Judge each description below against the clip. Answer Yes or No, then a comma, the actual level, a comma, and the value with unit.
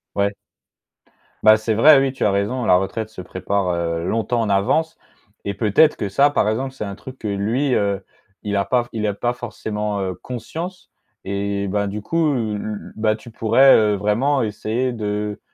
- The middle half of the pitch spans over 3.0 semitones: Yes, average, 3.5 semitones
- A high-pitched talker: No, low, 110 Hz